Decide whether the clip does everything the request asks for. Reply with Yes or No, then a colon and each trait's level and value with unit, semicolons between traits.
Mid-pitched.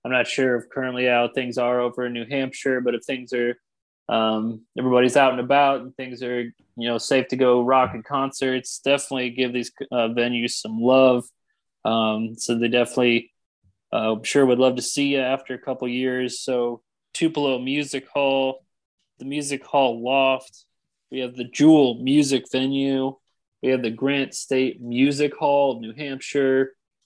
No: low, 130 Hz